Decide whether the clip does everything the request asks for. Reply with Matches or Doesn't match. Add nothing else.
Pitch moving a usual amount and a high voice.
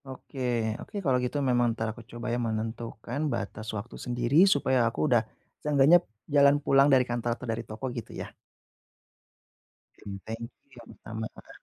Doesn't match